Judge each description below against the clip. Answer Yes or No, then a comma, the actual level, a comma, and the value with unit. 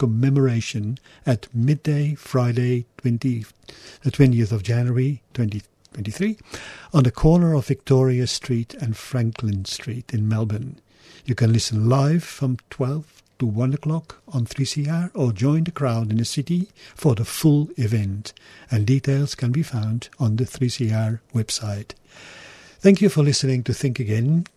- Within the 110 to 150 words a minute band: Yes, average, 145 wpm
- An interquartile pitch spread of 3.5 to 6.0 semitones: Yes, average, 3.9 semitones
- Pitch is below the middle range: Yes, low, 125 Hz